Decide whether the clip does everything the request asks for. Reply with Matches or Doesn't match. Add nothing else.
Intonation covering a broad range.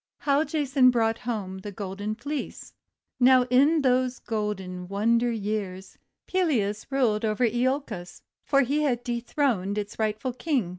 Doesn't match